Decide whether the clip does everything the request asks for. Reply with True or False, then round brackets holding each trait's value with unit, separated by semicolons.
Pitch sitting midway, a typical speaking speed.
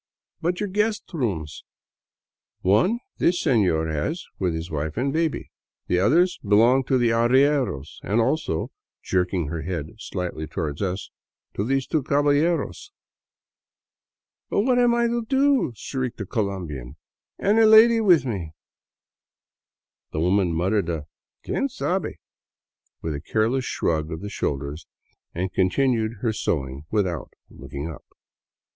False (110 Hz; 155 wpm)